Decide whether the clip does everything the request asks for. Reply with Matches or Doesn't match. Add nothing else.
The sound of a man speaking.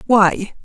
Doesn't match